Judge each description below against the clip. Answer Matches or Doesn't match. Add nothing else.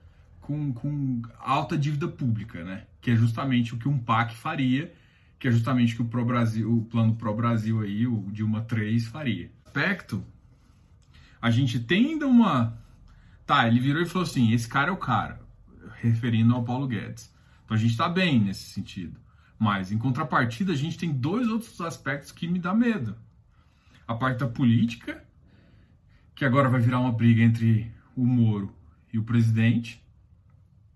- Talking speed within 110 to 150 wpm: Doesn't match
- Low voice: Matches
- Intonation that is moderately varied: Matches